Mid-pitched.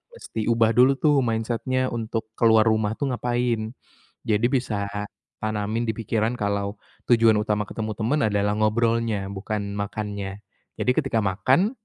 No: low, 110 Hz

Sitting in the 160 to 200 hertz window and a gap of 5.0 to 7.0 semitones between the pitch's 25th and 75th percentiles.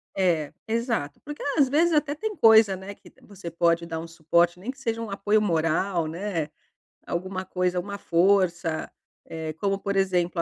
No: high, 190 Hz; average, 4.1 semitones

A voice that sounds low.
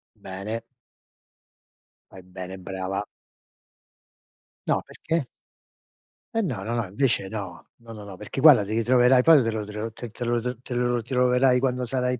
Yes: low, 115 Hz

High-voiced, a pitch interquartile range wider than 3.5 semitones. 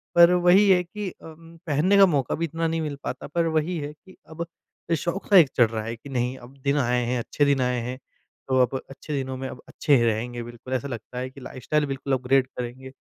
No: medium, 140 Hz; average, 4.6 semitones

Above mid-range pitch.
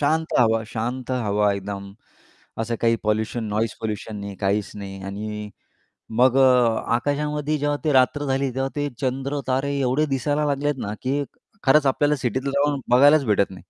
No: low, 130 Hz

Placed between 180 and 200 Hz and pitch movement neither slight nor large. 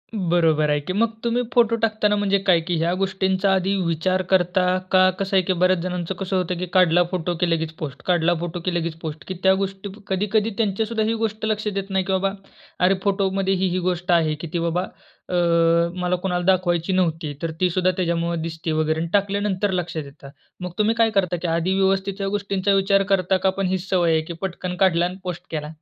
No: medium, 185 Hz; narrow, 2.3 semitones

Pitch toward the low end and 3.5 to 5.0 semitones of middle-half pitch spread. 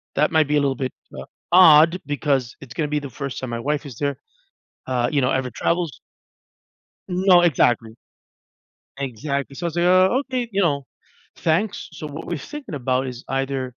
No: medium, 145 Hz; average, 4.5 semitones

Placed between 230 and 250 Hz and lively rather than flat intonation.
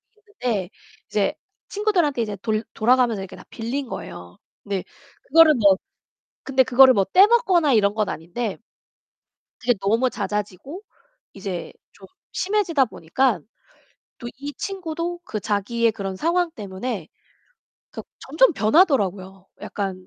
Yes: high, 235 Hz; wide, 7.7 semitones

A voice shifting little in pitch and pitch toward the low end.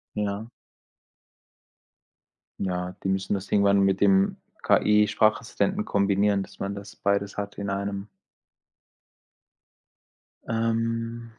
Yes: narrow, 1.8 semitones; low, 100 Hz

